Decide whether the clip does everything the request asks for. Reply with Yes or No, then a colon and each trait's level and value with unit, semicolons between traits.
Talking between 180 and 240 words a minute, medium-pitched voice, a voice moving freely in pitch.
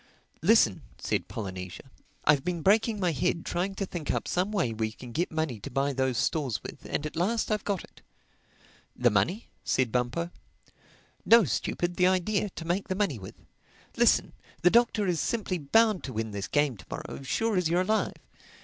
Yes: average, 185 wpm; medium, 170 Hz; wide, 7.4 semitones